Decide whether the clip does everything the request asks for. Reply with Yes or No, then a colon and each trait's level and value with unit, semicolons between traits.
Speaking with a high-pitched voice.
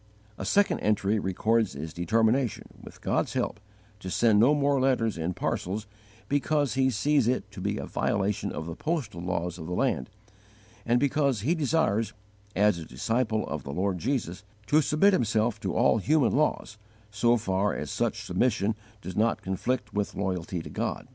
No: low, 110 Hz